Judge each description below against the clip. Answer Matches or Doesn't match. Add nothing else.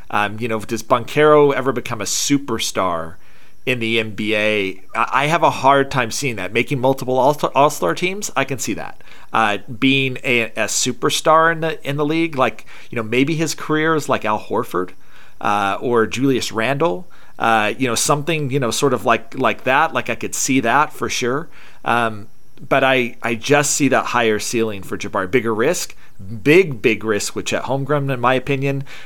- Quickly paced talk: Doesn't match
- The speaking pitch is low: Matches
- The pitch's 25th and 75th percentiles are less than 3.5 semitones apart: Doesn't match